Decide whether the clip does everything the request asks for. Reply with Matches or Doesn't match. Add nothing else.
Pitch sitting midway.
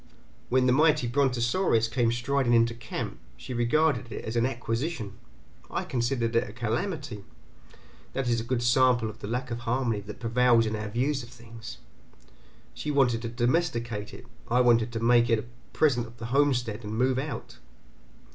Doesn't match